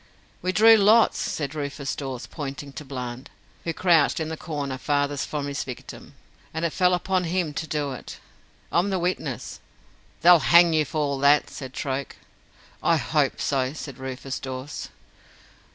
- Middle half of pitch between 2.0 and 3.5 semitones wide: No, average, 3.9 semitones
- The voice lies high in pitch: No, medium, 145 Hz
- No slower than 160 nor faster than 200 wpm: Yes, average, 165 wpm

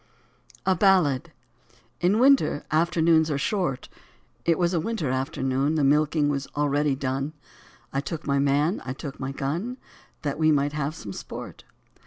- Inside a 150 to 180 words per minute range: Yes, average, 160 wpm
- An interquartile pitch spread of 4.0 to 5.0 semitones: No, average, 3.4 semitones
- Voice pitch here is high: No, medium, 150 Hz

